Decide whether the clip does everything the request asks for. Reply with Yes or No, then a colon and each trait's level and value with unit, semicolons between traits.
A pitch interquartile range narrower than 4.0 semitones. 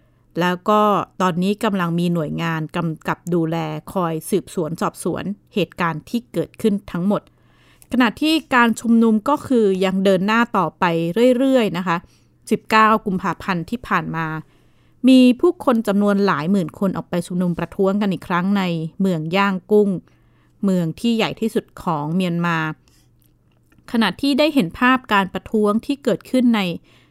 No: average, 4.5 semitones